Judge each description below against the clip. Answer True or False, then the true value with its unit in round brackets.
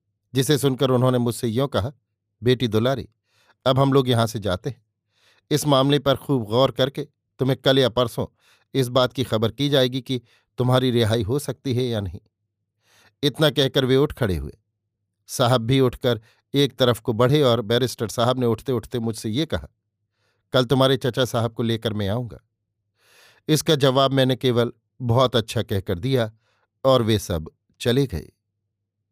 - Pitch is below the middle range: True (120 Hz)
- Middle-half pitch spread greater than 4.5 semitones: False (3.7 semitones)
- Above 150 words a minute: True (170 wpm)